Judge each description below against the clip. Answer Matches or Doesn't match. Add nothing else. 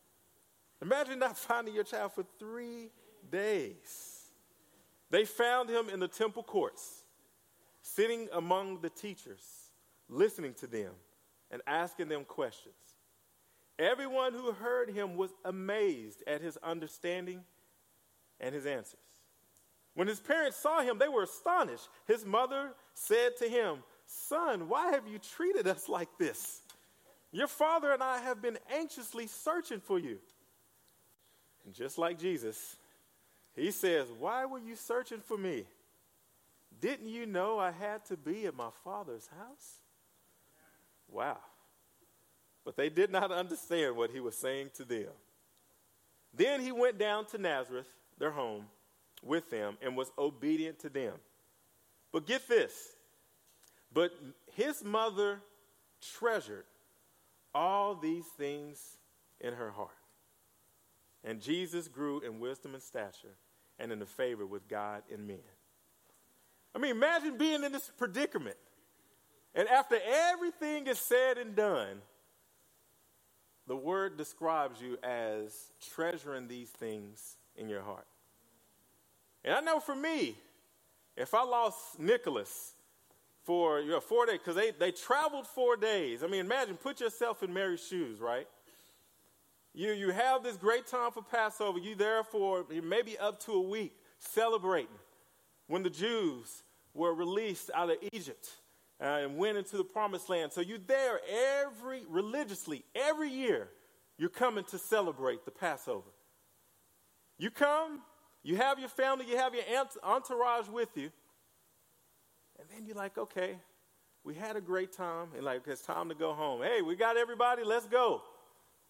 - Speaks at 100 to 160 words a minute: Matches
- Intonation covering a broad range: Matches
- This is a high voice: Matches